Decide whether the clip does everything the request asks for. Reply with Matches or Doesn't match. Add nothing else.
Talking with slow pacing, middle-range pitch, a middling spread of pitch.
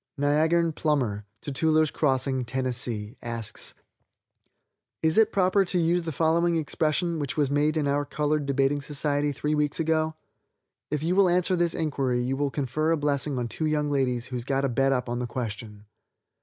Doesn't match